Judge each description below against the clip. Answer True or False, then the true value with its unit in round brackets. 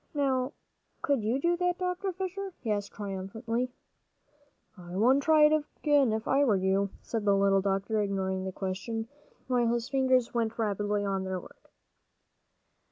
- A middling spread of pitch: False (5.8 semitones)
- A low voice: False (225 Hz)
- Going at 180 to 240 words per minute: False (160 wpm)